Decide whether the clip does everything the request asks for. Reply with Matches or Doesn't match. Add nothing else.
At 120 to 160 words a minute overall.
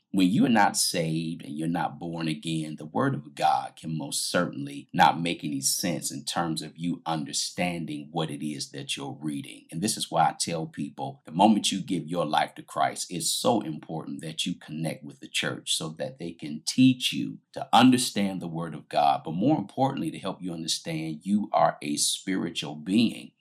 Doesn't match